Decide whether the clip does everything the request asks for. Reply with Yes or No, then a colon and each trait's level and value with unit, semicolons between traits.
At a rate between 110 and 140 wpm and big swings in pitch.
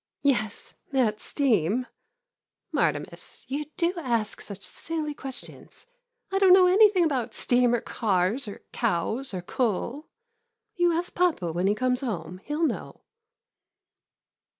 Yes: slow, 135 wpm; wide, 7.2 semitones